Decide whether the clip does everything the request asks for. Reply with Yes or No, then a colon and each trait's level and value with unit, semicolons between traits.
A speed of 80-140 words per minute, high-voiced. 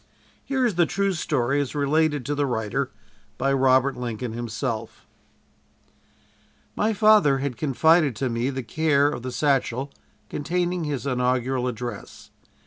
No: slow, 135 wpm; low, 135 Hz